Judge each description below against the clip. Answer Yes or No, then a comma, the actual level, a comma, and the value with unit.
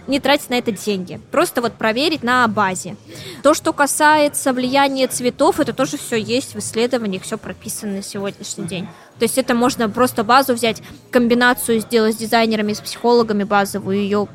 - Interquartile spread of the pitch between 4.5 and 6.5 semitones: No, average, 3.9 semitones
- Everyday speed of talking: No, fast, 170 wpm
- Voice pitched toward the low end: No, high, 235 Hz